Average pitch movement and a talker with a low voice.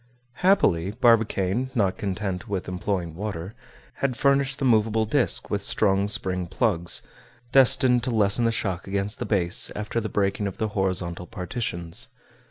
Yes: average, 4.0 semitones; low, 100 Hz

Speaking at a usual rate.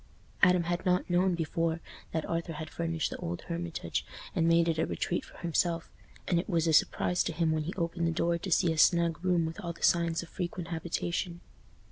No: fast, 215 wpm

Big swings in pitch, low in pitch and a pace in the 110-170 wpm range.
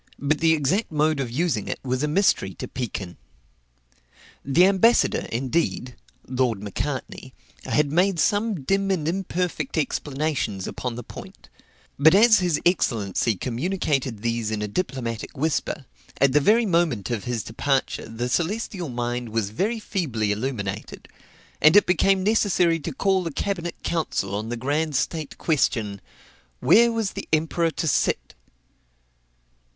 No: wide, 6.9 semitones; medium, 150 Hz; average, 145 wpm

